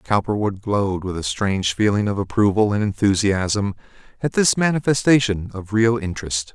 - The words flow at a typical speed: Yes, average, 145 wpm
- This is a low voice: Yes, low, 105 Hz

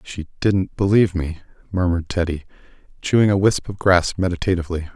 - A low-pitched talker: Yes, very low, 90 Hz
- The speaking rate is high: No, average, 145 wpm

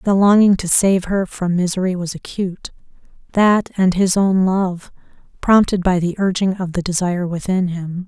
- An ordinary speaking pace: Yes, average, 170 wpm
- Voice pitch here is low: No, medium, 185 Hz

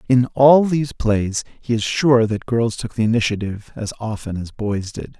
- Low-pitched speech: Yes, low, 115 Hz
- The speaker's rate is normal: Yes, average, 195 wpm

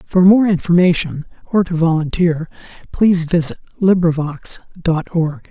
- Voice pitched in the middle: Yes, medium, 170 Hz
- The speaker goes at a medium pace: No, slow, 120 wpm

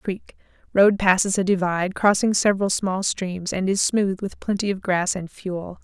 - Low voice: No, high, 190 Hz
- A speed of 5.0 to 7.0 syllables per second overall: No, 4.6 syllables/s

